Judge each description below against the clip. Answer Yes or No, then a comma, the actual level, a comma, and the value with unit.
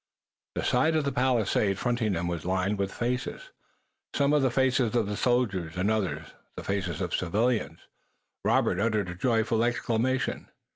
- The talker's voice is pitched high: No, low, 110 Hz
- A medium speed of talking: Yes, average, 150 wpm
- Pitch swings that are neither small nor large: Yes, average, 4.9 semitones